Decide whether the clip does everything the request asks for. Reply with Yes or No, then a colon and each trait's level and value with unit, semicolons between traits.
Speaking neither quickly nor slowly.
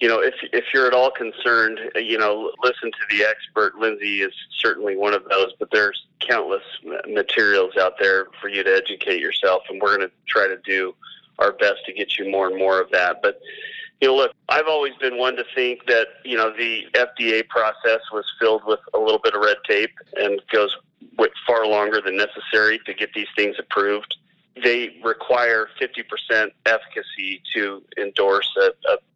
Yes: average, 190 wpm